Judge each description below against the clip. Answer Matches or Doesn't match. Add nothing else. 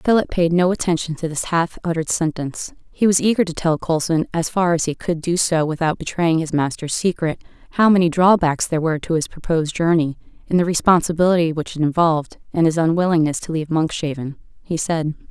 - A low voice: Doesn't match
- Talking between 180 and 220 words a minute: Matches